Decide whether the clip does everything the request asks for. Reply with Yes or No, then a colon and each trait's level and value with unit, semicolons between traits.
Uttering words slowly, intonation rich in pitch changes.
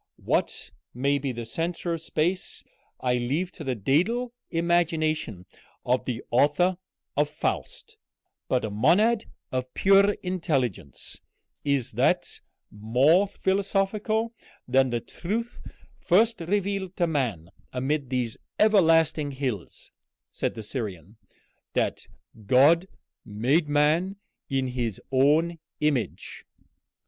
Yes: slow, 110 wpm; wide, 6.2 semitones